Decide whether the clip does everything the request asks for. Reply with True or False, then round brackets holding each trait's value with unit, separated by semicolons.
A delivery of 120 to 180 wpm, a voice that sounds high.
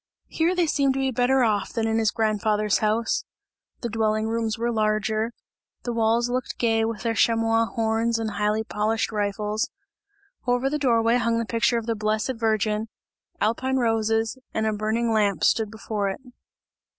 True (175 wpm; 225 Hz)